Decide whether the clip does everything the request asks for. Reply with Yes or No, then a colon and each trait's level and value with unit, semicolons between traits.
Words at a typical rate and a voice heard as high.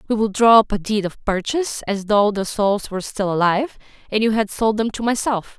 No: fast, 235 wpm; high, 210 Hz